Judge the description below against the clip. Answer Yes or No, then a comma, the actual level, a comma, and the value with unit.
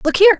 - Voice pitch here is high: Yes, very high, 385 Hz